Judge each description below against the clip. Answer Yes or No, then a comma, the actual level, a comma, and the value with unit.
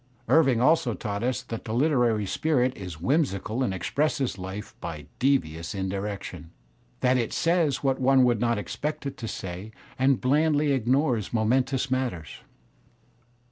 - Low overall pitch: Yes, low, 125 Hz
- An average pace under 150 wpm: Yes, average, 140 wpm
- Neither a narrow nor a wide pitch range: Yes, average, 4.7 semitones